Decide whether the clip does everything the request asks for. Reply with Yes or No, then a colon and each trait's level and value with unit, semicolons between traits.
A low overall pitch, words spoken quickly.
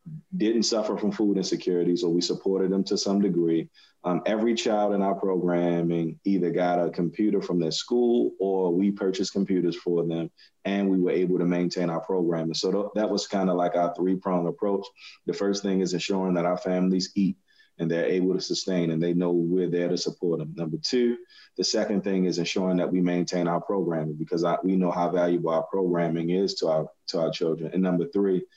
Yes: very low, 90 Hz; fast, 215 wpm